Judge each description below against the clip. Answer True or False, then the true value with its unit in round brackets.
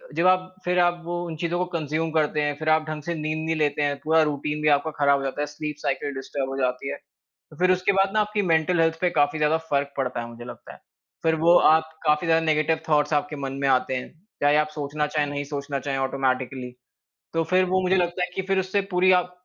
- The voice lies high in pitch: False (155 Hz)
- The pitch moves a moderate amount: True (3.3 semitones)